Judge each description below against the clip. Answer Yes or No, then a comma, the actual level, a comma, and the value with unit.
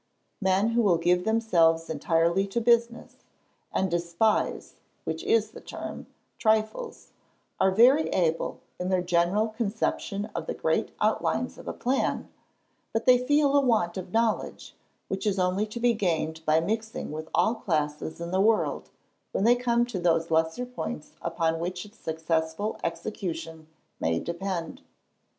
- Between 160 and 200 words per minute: No, average, 150 wpm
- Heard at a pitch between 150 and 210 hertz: Yes, high, 190 Hz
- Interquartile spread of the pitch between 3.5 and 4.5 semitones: No, average, 5.3 semitones